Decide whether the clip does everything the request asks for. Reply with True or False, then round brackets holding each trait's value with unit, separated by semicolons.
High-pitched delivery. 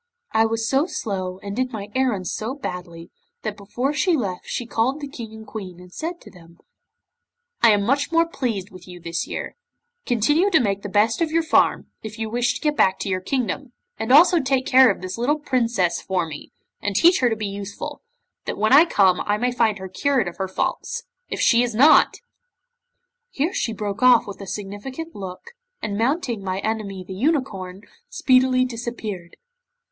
True (225 Hz)